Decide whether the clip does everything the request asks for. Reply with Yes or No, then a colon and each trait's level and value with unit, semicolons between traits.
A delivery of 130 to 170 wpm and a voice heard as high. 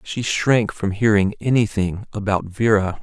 No: average, 140 wpm; low, 105 Hz